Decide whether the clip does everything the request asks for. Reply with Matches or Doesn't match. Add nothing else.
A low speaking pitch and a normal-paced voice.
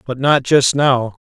Matches